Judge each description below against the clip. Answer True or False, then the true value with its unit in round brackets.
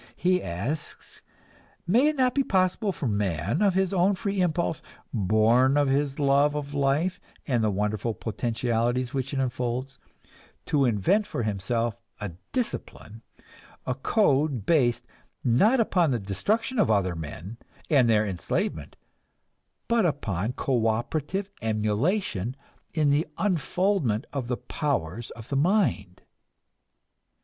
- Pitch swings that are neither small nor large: False (8.0 semitones)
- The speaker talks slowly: True (130 wpm)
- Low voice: True (130 Hz)